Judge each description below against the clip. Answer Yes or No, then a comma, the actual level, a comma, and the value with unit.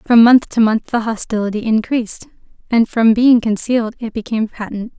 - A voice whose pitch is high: Yes, high, 225 Hz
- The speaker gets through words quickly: No, average, 170 wpm